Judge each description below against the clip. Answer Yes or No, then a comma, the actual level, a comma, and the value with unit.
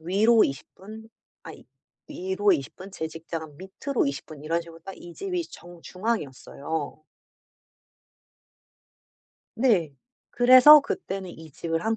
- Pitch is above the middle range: No, medium, 180 Hz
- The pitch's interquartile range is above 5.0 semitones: Yes, wide, 5.6 semitones